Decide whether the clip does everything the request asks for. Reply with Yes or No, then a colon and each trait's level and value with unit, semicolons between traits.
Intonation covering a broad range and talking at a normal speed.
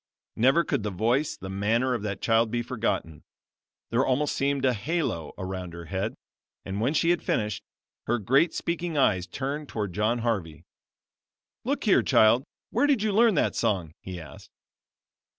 Yes: wide, 6.2 semitones; average, 170 wpm